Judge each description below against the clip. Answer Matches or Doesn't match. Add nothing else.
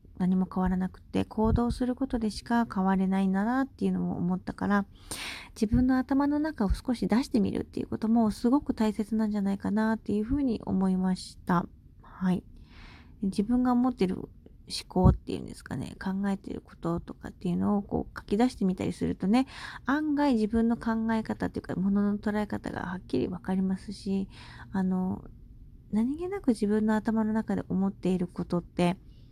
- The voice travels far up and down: Doesn't match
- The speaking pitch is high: Matches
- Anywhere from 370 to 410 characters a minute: Matches